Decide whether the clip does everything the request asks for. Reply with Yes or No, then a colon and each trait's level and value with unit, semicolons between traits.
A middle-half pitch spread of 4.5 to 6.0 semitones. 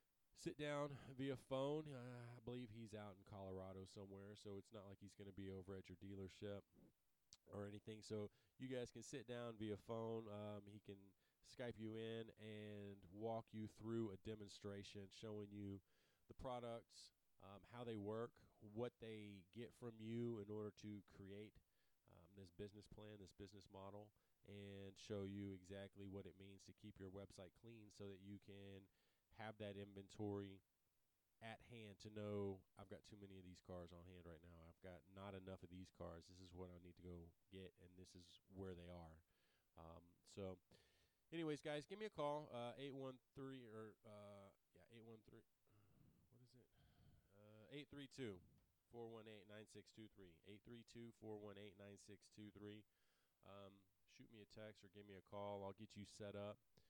No: average, 2.7 semitones